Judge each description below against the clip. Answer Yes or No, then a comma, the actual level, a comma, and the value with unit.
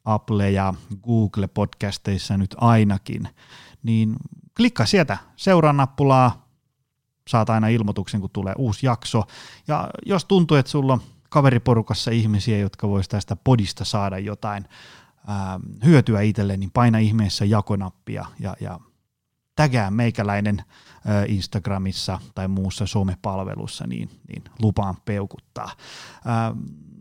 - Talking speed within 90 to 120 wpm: Yes, average, 115 wpm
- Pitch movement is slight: No, average, 3.5 semitones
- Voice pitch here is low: Yes, low, 110 Hz